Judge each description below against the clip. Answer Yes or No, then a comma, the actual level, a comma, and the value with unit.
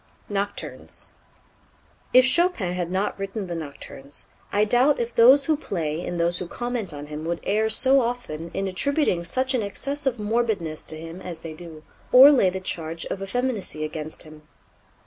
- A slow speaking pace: No, average, 175 wpm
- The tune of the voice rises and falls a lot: Yes, wide, 6.7 semitones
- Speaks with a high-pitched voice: Yes, high, 195 Hz